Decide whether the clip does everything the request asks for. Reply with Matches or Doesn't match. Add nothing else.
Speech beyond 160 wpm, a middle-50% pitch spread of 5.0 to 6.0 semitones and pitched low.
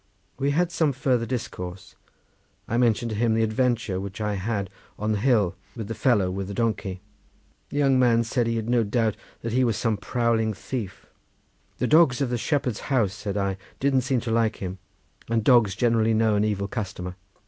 Doesn't match